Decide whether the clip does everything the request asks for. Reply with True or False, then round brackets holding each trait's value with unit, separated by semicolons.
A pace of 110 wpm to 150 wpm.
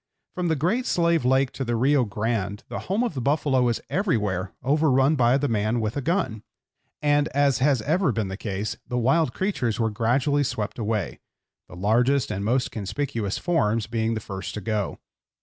False (185 wpm)